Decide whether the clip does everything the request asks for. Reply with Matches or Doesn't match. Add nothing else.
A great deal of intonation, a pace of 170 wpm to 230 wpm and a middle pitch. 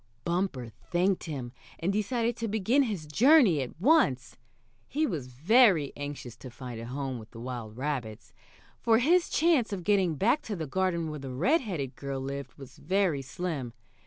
Matches